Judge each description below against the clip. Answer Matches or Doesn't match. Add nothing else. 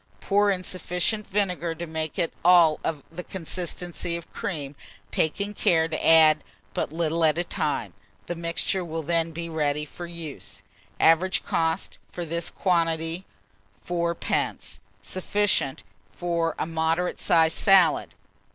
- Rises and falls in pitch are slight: Matches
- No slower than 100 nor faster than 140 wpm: Matches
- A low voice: Doesn't match